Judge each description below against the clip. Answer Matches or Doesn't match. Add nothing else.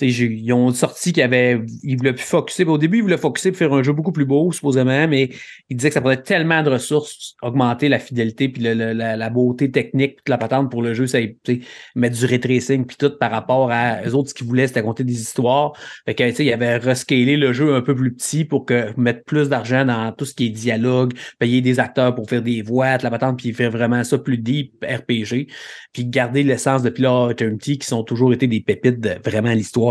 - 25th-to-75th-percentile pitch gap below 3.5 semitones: Matches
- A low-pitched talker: Matches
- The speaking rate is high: Matches